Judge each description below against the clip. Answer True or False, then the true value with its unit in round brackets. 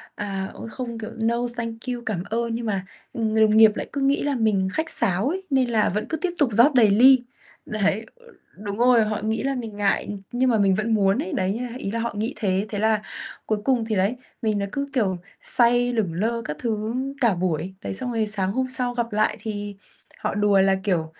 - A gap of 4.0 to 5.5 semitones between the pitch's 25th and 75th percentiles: False (3.2 semitones)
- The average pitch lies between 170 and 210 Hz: False (220 Hz)